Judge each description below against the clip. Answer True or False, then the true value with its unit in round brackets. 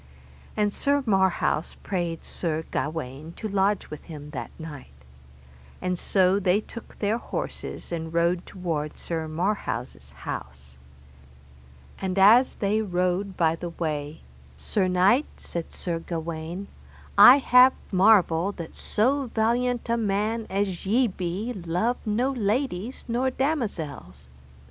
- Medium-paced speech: False (125 wpm)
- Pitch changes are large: False (4.9 semitones)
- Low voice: False (190 Hz)